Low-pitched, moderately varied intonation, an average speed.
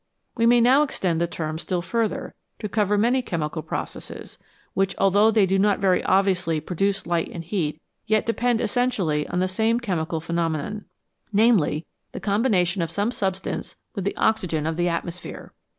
No: high, 190 Hz; average, 4.4 semitones; average, 165 wpm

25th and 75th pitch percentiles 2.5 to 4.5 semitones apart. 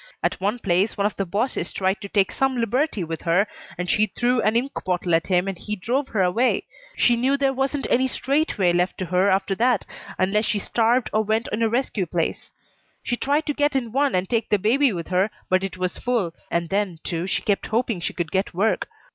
No: average, 4.9 semitones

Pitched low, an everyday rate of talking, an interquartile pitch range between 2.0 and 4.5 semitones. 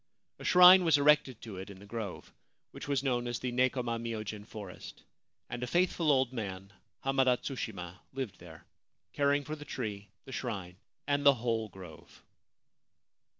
No: low, 120 Hz; average, 160 wpm; average, 5.3 semitones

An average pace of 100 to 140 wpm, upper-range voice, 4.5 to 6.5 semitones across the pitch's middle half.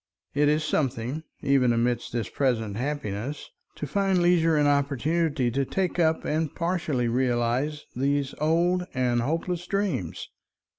No: slow, 135 wpm; medium, 145 Hz; average, 4.9 semitones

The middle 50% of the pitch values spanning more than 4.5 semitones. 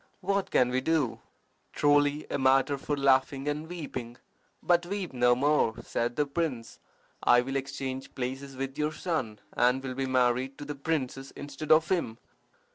No: average, 2.7 semitones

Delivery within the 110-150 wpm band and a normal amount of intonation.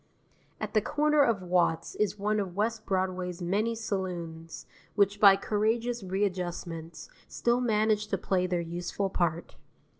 Yes: average, 140 wpm; average, 3.3 semitones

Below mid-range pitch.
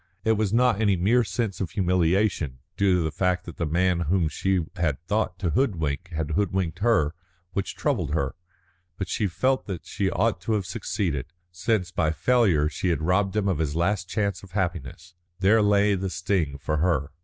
Yes: very low, 90 Hz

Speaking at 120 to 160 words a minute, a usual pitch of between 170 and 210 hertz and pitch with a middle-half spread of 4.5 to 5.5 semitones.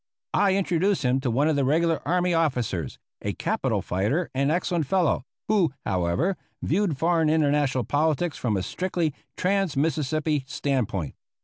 No: average, 150 wpm; medium, 155 Hz; average, 5.0 semitones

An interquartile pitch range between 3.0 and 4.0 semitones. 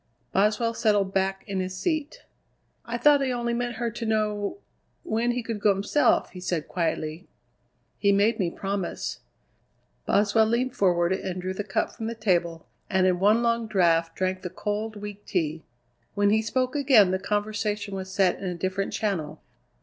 Yes: average, 3.4 semitones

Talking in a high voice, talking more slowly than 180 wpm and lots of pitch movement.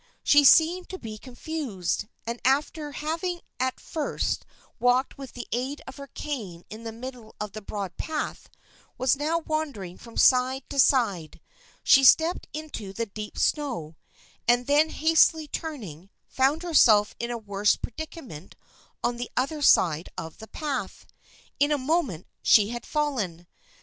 Yes: very high, 255 Hz; average, 155 wpm; wide, 5.8 semitones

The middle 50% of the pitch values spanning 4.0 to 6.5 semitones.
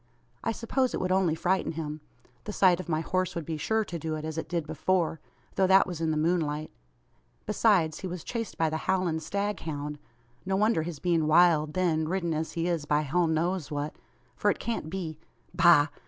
No: average, 3.0 semitones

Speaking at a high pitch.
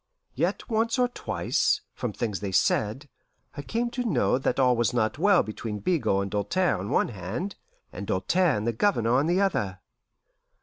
No: low, 125 Hz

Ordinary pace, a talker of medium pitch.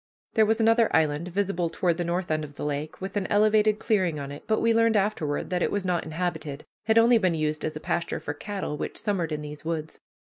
No: fast, 240 wpm; medium, 180 Hz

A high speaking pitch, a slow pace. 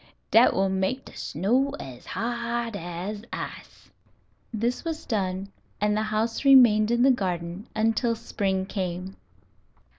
Yes: high, 215 Hz; slow, 130 wpm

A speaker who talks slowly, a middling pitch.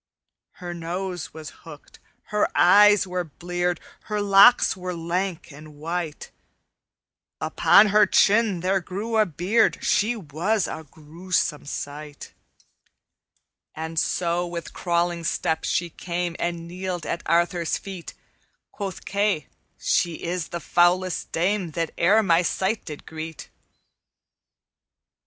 Yes: slow, 120 wpm; medium, 175 Hz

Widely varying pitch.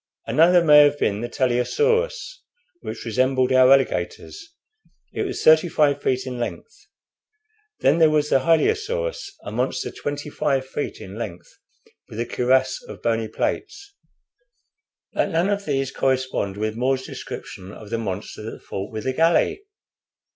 Yes: wide, 5.7 semitones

